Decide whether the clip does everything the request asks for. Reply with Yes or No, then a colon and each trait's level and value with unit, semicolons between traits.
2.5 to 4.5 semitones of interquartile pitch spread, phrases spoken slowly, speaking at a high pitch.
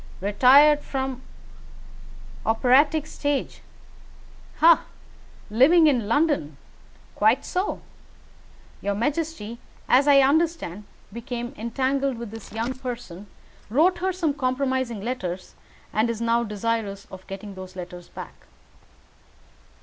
No: average, 5.2 semitones; slow, 105 wpm; high, 245 Hz